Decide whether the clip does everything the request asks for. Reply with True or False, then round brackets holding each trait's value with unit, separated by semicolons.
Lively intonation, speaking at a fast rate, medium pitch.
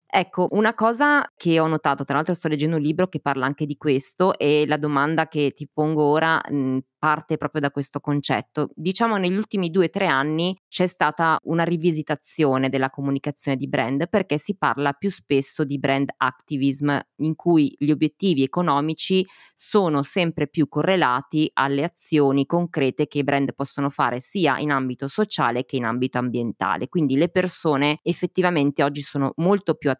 False (3.5 semitones; 175 wpm; 150 Hz)